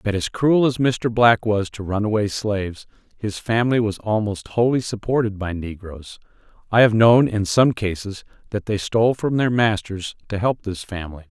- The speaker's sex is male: Yes, male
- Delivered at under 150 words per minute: No, average, 180 wpm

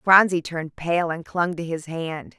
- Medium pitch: Yes, medium, 170 Hz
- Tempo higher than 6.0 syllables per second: No, 4.4 syllables/s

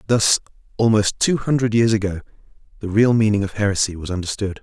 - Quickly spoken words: No, average, 170 wpm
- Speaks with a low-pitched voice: Yes, low, 105 Hz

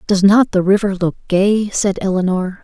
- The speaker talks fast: No, average, 180 wpm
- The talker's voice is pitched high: Yes, high, 195 Hz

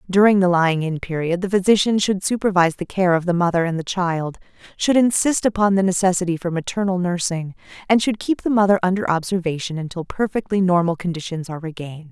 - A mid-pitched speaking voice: Yes, medium, 180 Hz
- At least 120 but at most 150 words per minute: No, average, 190 wpm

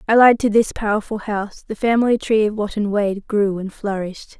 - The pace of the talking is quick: No, average, 190 wpm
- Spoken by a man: No, female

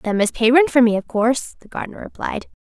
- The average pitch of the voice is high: Yes, high, 240 Hz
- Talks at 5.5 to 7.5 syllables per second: Yes, 6.1 syllables/s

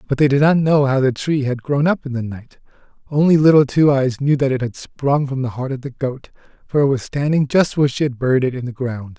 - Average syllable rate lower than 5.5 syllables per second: No, 5.8 syllables/s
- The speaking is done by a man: Yes, male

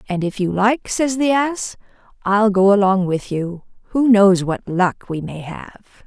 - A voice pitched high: Yes, high, 200 Hz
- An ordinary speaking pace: Yes, average, 190 wpm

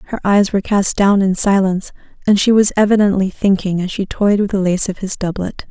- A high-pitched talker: Yes, high, 195 Hz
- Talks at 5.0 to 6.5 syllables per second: Yes, 5.8 syllables/s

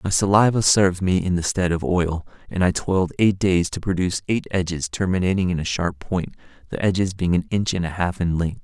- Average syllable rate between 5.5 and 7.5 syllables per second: Yes, 5.8 syllables/s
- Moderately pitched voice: No, very low, 90 Hz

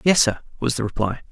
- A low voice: Yes, low, 125 Hz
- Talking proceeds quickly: Yes, fast, 230 wpm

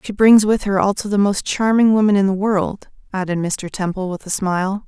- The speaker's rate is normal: No, fast, 220 wpm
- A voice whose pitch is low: No, high, 200 Hz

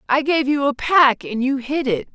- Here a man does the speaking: No, female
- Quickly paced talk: Yes, fast, 250 wpm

